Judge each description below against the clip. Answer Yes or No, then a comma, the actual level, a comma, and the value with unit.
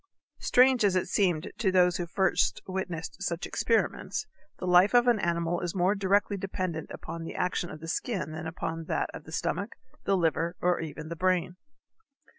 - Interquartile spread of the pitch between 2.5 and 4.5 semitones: Yes, average, 2.8 semitones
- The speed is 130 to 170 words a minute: No, average, 185 wpm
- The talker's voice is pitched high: No, medium, 180 Hz